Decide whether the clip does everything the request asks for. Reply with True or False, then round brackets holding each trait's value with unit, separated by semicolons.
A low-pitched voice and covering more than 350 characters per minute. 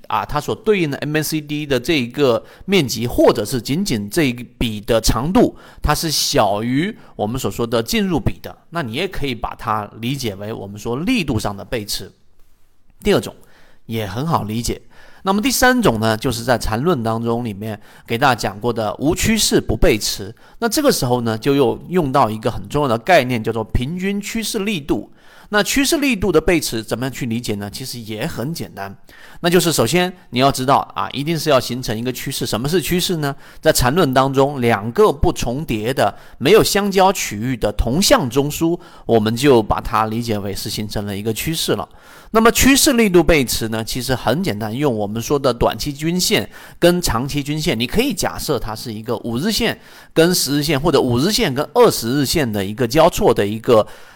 False (130 Hz; 295 characters per minute)